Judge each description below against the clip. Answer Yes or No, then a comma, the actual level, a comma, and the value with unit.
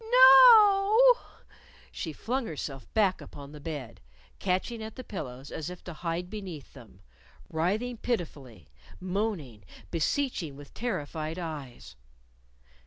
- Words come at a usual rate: No, slow, 125 wpm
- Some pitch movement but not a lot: No, wide, 8.4 semitones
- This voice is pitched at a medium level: Yes, medium, 180 Hz